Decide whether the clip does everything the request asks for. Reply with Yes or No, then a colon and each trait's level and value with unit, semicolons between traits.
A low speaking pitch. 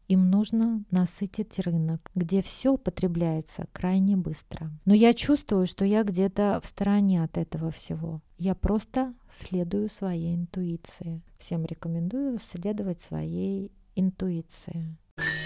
No: medium, 185 Hz